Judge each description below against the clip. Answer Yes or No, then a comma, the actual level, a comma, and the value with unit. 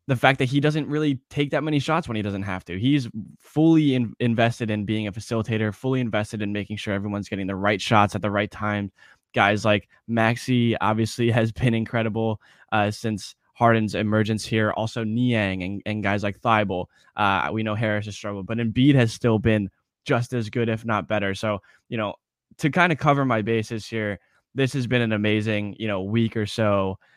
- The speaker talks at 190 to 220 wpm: Yes, fast, 205 wpm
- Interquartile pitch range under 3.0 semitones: Yes, narrow, 2.5 semitones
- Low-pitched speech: Yes, low, 110 Hz